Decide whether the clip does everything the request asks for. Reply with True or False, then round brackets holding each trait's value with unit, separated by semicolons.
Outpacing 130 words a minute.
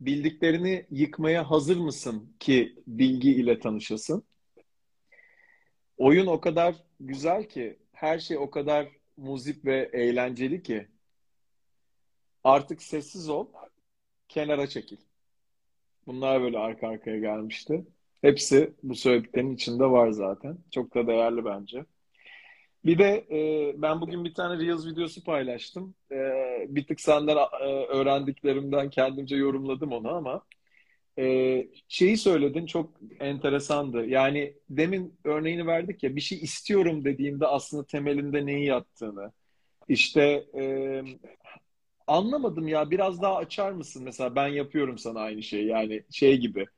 False (115 wpm)